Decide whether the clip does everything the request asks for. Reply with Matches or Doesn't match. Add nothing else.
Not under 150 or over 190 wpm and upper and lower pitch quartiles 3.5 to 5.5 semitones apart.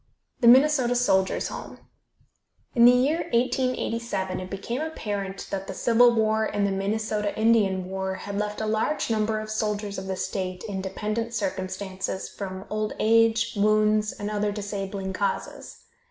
Doesn't match